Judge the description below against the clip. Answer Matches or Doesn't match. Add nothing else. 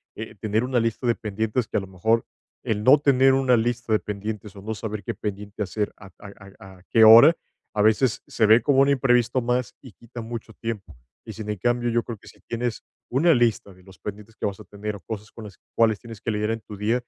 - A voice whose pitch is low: Matches